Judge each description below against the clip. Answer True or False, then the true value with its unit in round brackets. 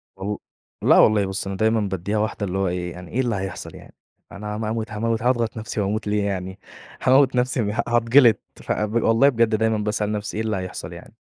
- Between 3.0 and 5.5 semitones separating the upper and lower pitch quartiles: False (2.6 semitones)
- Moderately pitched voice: False (105 Hz)